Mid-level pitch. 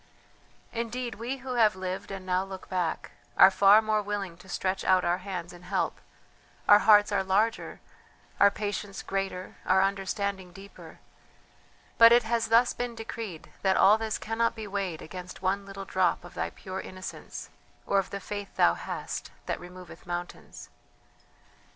No: high, 195 Hz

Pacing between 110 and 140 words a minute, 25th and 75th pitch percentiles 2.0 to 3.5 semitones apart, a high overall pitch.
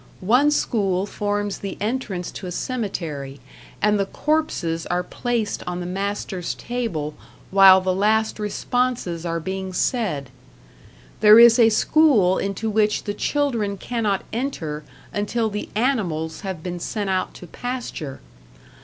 No: slow, 135 wpm; average, 4.2 semitones; high, 200 Hz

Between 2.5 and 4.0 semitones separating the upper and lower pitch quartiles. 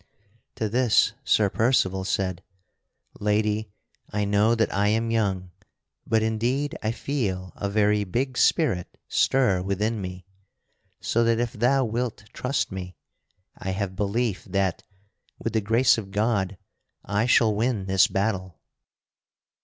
Yes: average, 3.1 semitones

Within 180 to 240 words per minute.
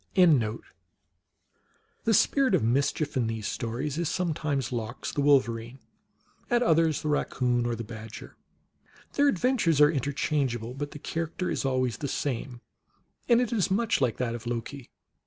No: average, 150 wpm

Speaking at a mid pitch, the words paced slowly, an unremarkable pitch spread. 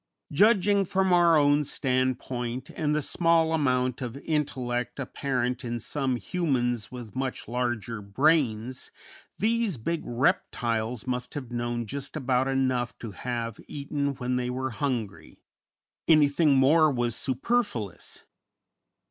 No: low, 130 Hz; slow, 125 wpm; average, 3.7 semitones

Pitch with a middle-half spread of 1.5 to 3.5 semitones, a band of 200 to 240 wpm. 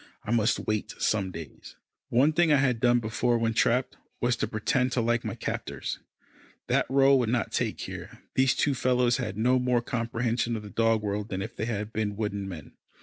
Yes: average, 2.7 semitones; fast, 205 wpm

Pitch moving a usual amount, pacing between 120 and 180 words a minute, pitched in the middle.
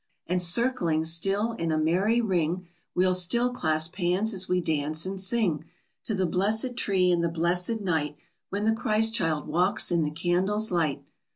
Yes: average, 4.2 semitones; average, 175 wpm; medium, 180 Hz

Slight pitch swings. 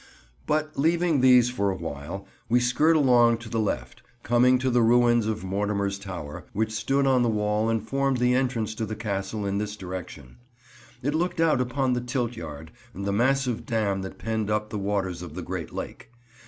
No: average, 4.1 semitones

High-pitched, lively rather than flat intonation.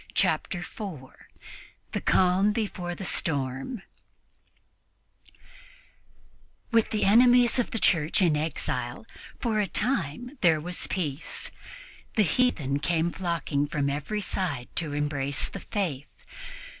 No: medium, 175 Hz; wide, 6.1 semitones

